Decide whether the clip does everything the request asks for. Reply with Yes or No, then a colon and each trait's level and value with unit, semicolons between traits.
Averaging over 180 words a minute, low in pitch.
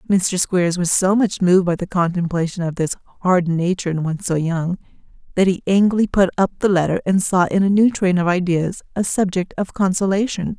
No: fast, 205 wpm; medium, 185 Hz